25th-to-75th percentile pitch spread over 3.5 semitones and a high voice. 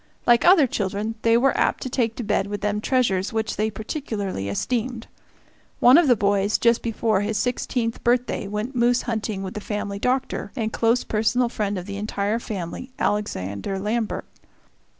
No: average, 2.9 semitones; high, 220 Hz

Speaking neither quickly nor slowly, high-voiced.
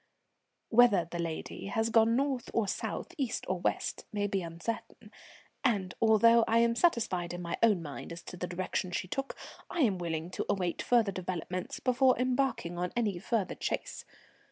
Yes: average, 175 wpm; high, 205 Hz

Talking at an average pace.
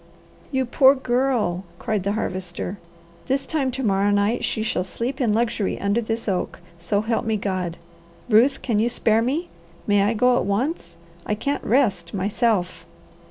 Yes: average, 165 wpm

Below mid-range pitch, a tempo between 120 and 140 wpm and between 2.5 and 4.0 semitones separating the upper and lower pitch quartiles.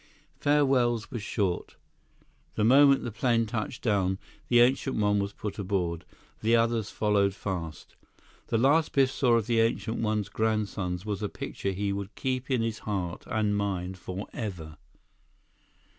No: low, 105 Hz; average, 150 wpm; average, 3.1 semitones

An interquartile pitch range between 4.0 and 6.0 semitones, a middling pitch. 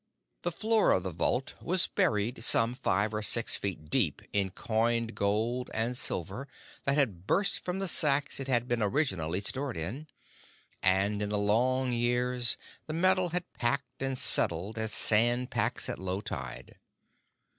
No: average, 4.9 semitones; low, 120 Hz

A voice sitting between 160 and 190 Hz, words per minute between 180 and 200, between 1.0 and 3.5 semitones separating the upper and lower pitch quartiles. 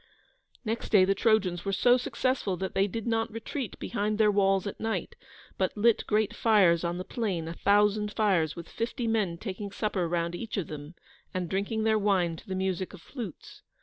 No: high, 200 Hz; average, 195 wpm; average, 3.2 semitones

